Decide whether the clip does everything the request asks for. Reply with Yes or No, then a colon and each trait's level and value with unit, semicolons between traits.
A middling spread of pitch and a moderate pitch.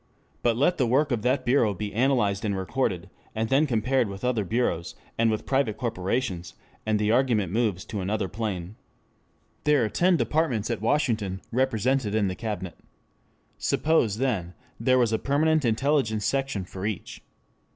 No: average, 4.5 semitones; low, 115 Hz